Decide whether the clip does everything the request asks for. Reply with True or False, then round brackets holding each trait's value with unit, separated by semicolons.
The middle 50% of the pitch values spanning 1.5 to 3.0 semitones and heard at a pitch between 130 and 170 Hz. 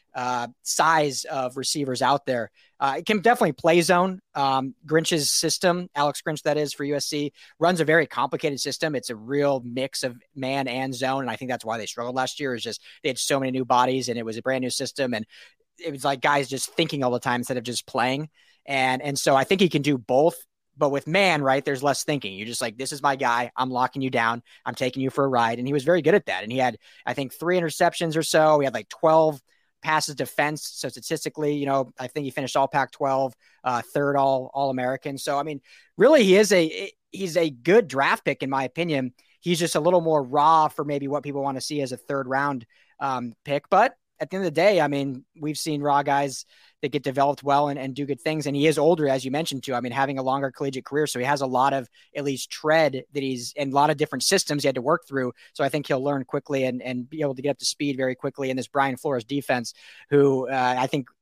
True (2.7 semitones; 140 Hz)